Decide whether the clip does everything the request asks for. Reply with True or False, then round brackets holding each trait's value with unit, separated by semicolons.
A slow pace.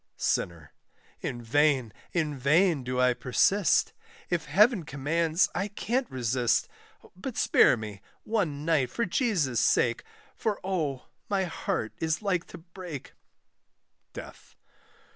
True (120 wpm)